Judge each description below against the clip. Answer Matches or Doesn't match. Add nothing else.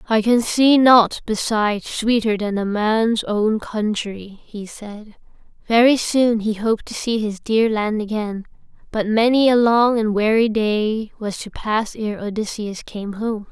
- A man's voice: Doesn't match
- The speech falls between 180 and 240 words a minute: Doesn't match